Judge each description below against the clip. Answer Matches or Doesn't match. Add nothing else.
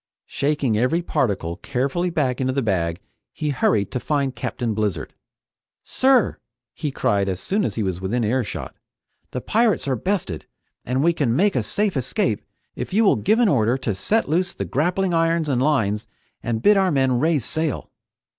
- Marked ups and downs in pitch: Matches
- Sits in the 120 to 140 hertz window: Matches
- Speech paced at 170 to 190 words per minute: Matches